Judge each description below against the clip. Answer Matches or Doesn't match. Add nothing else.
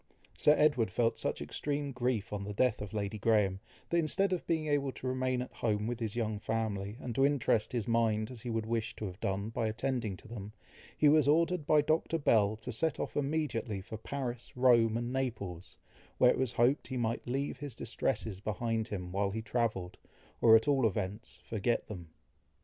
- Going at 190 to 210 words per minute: Matches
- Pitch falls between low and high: Doesn't match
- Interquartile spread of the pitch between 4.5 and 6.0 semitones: Doesn't match